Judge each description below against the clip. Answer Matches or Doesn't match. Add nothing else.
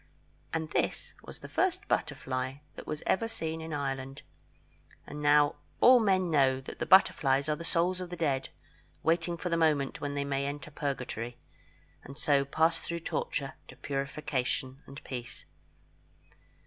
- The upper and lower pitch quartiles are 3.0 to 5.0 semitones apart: Matches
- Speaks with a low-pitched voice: Doesn't match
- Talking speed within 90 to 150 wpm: Doesn't match